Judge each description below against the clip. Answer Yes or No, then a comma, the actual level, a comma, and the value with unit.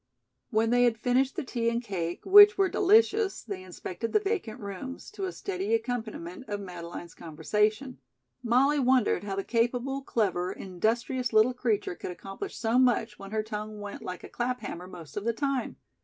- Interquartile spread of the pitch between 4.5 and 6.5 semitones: Yes, average, 4.8 semitones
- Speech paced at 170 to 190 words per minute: Yes, average, 180 wpm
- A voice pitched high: Yes, high, 230 Hz